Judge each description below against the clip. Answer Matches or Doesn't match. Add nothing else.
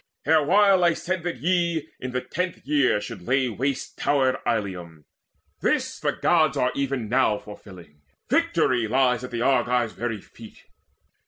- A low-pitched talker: Matches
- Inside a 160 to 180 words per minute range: Doesn't match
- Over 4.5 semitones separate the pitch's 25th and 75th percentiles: Matches